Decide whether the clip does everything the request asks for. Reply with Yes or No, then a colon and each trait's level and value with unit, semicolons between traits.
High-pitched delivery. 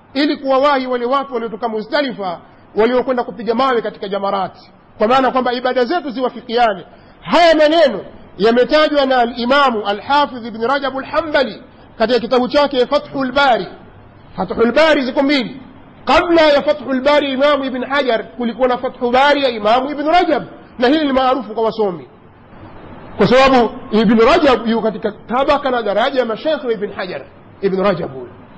Yes: very high, 250 Hz